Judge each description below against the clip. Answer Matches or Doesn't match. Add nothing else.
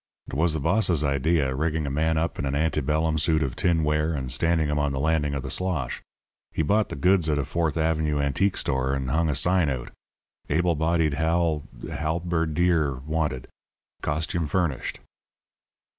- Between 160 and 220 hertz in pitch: Doesn't match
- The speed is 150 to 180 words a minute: Matches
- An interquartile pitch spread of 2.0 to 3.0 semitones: Matches